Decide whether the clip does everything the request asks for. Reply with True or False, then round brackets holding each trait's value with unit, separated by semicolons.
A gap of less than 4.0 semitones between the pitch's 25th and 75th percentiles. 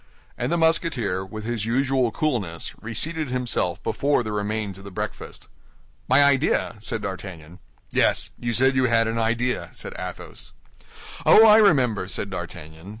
False (5.2 semitones)